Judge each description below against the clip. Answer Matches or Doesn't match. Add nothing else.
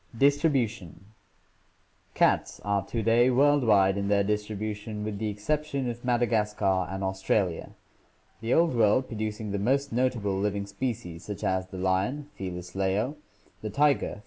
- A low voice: Matches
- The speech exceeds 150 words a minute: Doesn't match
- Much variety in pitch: Doesn't match